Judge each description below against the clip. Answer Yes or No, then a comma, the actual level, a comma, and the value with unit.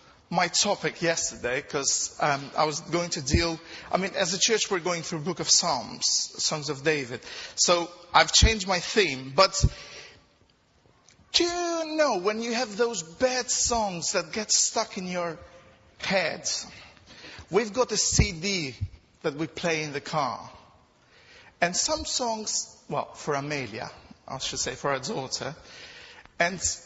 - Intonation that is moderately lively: No, wide, 6.0 semitones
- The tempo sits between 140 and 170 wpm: Yes, average, 155 wpm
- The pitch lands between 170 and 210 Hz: Yes, high, 190 Hz